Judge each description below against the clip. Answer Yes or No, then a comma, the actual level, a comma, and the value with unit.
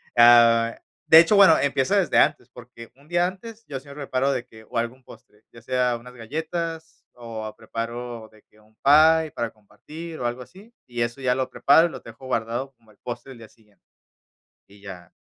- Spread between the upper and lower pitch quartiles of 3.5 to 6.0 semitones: Yes, average, 4.8 semitones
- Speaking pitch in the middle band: No, low, 125 Hz